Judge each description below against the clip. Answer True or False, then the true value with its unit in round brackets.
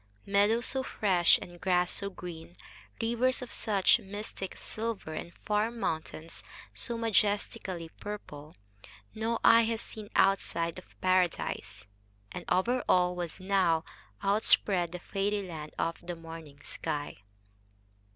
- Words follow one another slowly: True (125 wpm)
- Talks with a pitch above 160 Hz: True (190 Hz)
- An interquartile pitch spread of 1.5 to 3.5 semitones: False (3.9 semitones)